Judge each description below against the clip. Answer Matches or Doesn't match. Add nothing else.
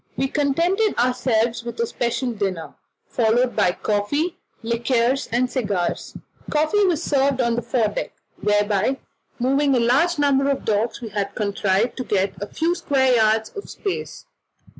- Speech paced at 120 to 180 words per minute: Matches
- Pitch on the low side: Doesn't match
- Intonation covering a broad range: Doesn't match